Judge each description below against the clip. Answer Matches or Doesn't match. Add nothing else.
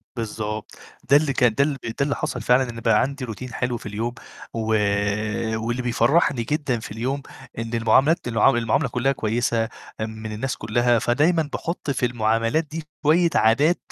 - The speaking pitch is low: Matches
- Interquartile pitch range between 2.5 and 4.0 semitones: Matches